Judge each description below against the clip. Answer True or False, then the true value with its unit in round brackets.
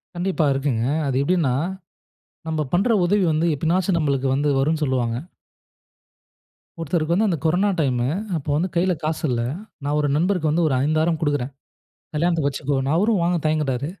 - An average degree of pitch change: True (3.7 semitones)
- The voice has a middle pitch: True (155 Hz)